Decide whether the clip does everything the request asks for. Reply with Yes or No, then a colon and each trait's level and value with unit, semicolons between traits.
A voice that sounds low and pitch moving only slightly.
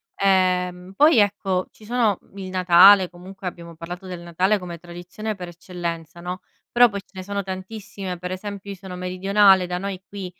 No: medium, 185 Hz; narrow, 1.9 semitones